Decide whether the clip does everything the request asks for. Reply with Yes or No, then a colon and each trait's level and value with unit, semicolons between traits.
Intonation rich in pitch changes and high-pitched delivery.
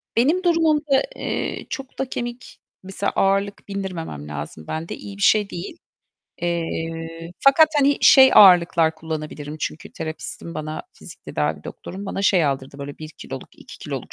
No: wide, 7.1 semitones; medium, 180 Hz